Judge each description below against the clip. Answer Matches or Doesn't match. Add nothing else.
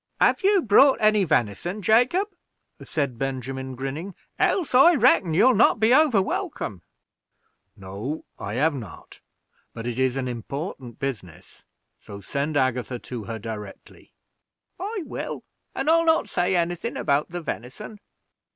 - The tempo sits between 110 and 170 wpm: Matches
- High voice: Doesn't match